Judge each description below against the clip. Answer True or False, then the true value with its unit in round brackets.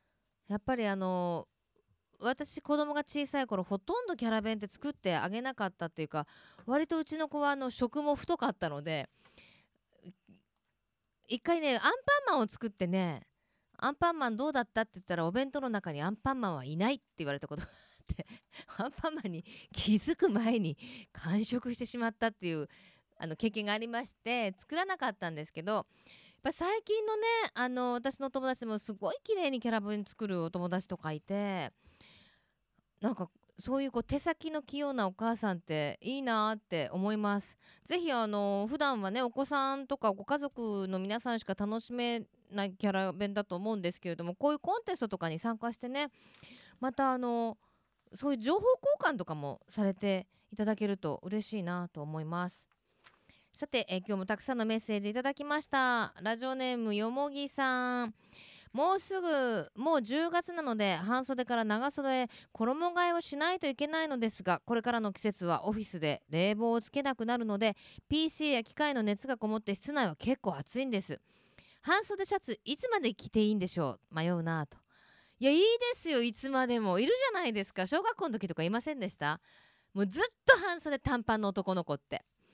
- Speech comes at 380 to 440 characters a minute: False (370 characters per minute)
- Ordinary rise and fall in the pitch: False (6.2 semitones)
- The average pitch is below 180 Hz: False (230 Hz)